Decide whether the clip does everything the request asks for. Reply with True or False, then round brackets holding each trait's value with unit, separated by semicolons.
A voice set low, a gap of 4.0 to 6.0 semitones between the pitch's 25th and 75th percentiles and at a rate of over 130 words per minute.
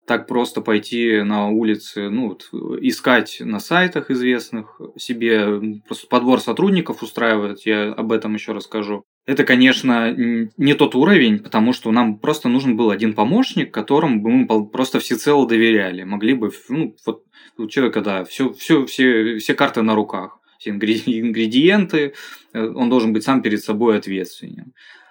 True (115 Hz; 4.6 semitones; 150 wpm)